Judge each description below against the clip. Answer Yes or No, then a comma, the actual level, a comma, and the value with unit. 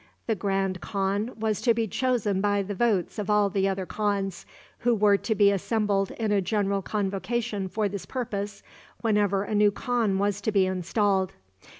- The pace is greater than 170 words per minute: Yes, average, 180 wpm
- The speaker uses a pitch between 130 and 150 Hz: No, high, 205 Hz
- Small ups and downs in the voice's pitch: Yes, narrow, 1.8 semitones